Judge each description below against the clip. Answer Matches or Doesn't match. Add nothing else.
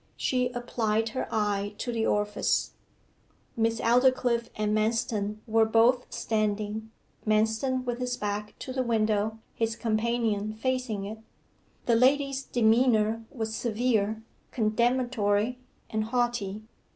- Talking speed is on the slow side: Matches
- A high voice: Matches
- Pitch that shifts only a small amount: Matches